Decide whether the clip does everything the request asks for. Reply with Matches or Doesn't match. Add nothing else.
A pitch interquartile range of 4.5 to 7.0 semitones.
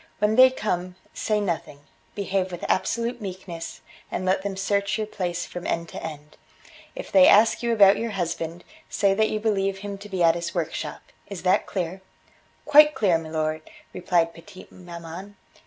Doesn't match